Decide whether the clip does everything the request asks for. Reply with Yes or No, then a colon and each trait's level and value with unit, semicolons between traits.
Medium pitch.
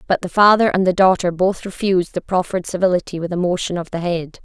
Yes: medium, 180 Hz